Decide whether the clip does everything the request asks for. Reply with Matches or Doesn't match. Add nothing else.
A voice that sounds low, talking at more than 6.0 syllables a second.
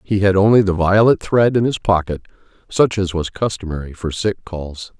Doesn't match